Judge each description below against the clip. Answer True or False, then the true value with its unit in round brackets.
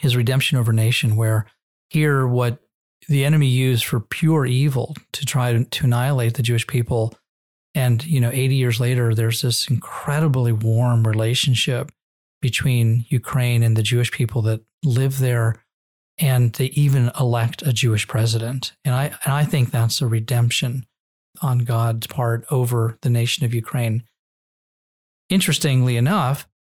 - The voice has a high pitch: False (125 Hz)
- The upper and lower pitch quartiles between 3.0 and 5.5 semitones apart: False (2.5 semitones)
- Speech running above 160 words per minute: False (150 wpm)